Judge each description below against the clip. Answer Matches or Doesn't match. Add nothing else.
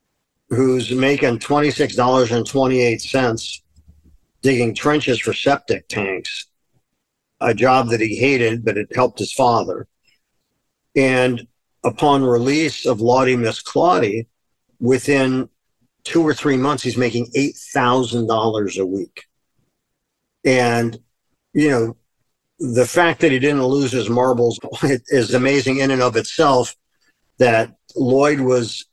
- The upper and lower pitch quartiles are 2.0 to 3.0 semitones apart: Matches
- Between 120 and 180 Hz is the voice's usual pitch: Matches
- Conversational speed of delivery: Doesn't match